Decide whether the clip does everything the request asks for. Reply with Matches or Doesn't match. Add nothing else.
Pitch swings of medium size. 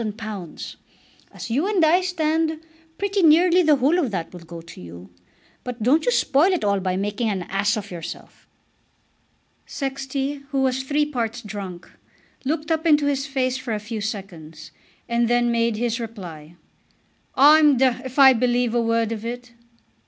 Doesn't match